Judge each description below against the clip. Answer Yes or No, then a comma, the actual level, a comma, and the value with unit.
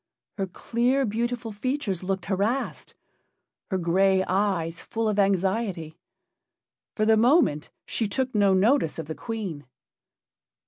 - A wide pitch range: No, average, 3.6 semitones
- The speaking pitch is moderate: No, high, 200 Hz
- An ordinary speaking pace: No, slow, 125 wpm